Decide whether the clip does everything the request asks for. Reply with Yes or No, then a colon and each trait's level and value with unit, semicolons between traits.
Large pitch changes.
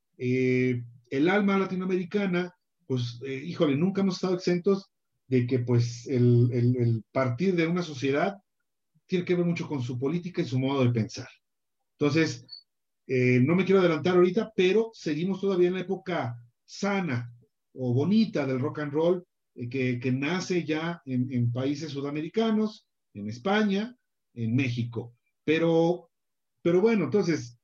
Yes: wide, 6.4 semitones